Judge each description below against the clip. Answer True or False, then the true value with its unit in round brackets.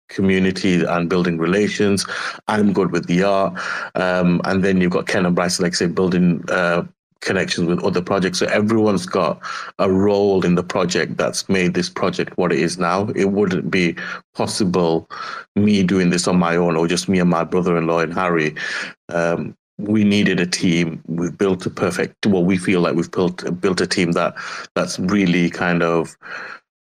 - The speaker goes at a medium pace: True (185 wpm)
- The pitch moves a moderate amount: False (2.0 semitones)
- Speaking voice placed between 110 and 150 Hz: False (90 Hz)